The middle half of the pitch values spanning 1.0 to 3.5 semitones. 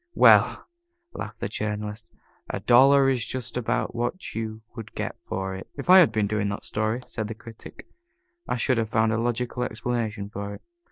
Yes: narrow, 2.5 semitones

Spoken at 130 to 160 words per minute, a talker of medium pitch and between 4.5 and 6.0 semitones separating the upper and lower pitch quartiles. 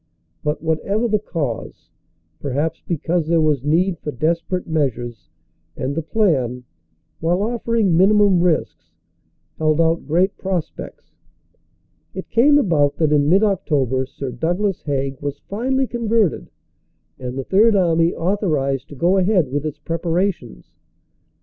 Yes: slow, 135 wpm; medium, 165 Hz; average, 5.2 semitones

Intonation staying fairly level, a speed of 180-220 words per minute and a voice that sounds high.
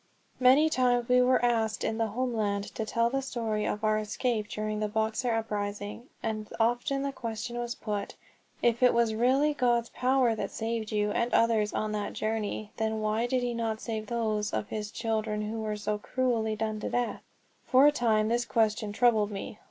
Yes: narrow, 2.1 semitones; average, 190 wpm; high, 225 Hz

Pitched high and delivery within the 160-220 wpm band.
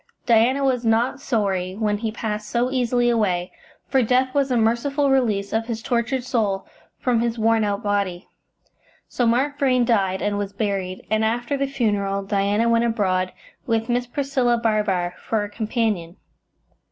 Yes: high, 225 Hz; average, 165 wpm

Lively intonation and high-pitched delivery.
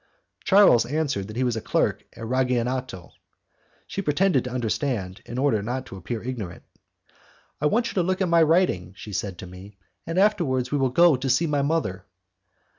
No: wide, 6.8 semitones; low, 130 Hz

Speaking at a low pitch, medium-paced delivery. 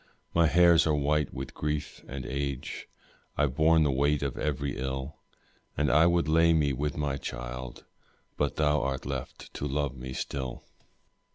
Yes: very low, 70 Hz; average, 165 wpm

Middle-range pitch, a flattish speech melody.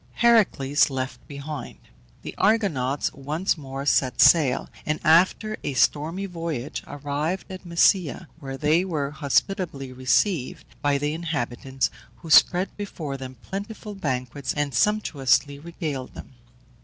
No: medium, 150 Hz; average, 4.7 semitones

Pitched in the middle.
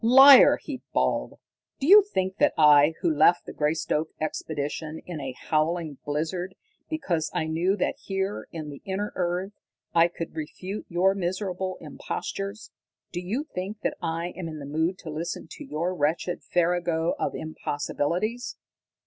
Yes: medium, 175 Hz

